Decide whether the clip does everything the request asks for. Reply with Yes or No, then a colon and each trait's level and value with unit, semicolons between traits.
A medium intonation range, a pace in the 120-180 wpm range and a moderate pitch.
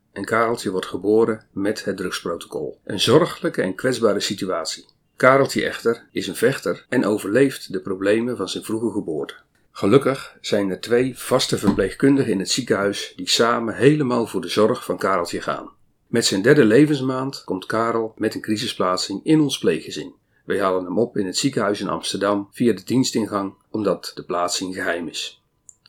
No: average, 3.6 semitones; average, 165 wpm; low, 110 Hz